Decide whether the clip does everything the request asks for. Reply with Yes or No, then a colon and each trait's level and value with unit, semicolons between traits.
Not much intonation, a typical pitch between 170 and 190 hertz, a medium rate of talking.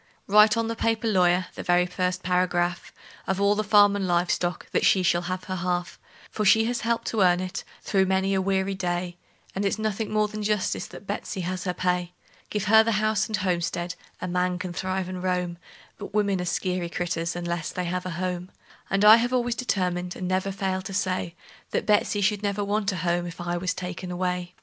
No: narrow, 2.3 semitones; medium, 185 Hz; fast, 215 wpm